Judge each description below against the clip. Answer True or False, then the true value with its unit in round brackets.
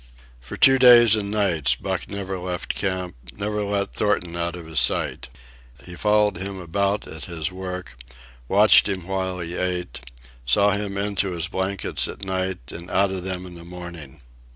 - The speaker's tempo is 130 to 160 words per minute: False (175 wpm)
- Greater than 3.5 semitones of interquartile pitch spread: False (2.4 semitones)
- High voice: False (95 Hz)